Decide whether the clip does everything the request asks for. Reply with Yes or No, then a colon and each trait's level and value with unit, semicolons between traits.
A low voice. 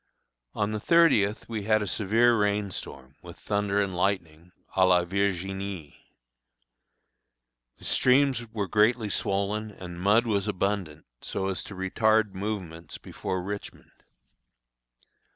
Yes: low, 100 Hz